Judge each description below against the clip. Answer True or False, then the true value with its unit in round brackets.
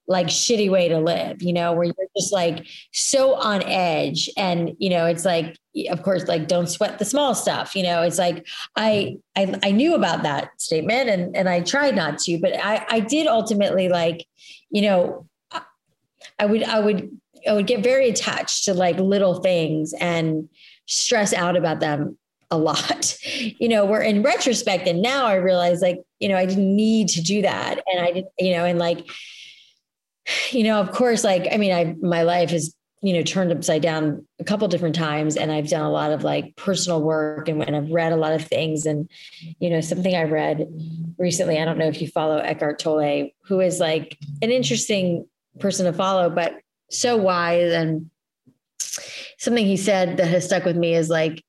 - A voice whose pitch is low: False (180 Hz)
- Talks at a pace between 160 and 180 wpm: False (200 wpm)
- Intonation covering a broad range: False (3.5 semitones)